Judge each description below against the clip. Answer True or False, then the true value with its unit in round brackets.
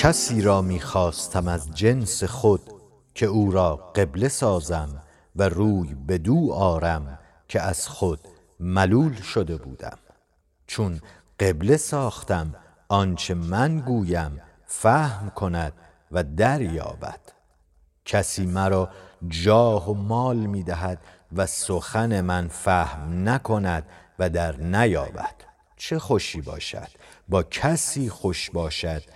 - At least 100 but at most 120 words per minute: True (110 wpm)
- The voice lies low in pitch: True (95 Hz)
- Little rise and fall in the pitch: False (4.0 semitones)